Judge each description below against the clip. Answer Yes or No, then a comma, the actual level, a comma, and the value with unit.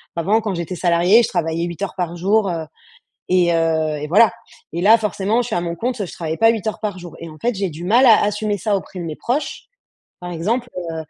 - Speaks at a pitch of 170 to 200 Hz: Yes, medium, 185 Hz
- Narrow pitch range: No, average, 4.3 semitones